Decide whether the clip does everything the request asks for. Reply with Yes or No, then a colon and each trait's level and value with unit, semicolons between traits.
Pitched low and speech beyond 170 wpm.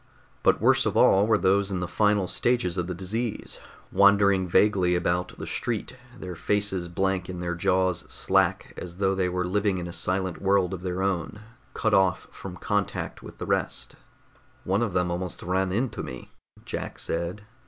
Yes: very low, 95 Hz; average, 180 wpm